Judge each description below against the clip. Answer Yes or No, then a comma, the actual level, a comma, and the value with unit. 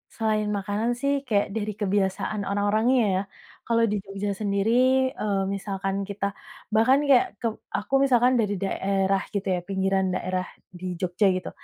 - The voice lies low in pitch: No, high, 205 Hz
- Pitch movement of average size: No, narrow, 2.2 semitones